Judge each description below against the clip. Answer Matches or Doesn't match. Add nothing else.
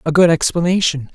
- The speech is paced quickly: Doesn't match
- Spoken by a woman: Doesn't match